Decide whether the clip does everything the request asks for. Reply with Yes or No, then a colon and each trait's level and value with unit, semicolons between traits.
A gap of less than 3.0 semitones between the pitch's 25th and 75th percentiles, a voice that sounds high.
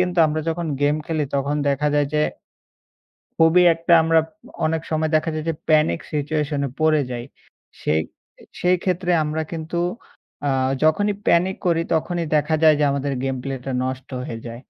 No: narrow, 2.5 semitones; medium, 155 Hz